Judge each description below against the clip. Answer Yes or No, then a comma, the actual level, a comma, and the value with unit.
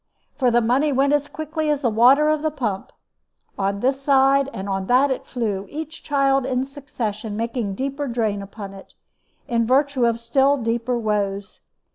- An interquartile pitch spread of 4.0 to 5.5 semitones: Yes, average, 4.3 semitones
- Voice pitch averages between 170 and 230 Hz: No, very high, 250 Hz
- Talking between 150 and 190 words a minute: Yes, average, 175 wpm